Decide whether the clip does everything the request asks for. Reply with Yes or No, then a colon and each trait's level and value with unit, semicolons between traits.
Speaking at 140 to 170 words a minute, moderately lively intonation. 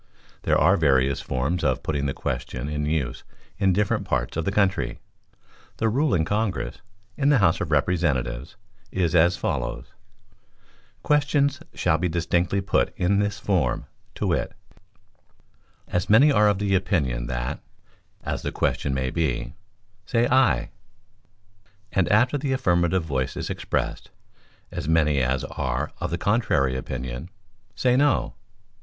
No: average, 145 wpm; wide, 7.1 semitones